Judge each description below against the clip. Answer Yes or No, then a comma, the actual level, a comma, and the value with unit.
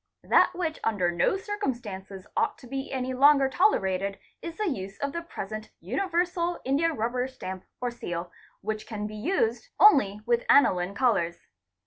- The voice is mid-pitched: No, high, 245 Hz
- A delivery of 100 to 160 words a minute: Yes, average, 155 wpm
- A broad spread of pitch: Yes, wide, 7.9 semitones